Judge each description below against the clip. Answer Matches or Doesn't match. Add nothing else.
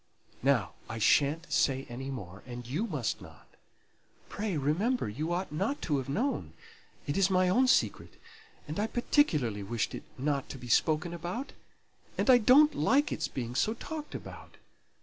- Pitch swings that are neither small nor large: Doesn't match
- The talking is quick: Doesn't match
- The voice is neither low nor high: Matches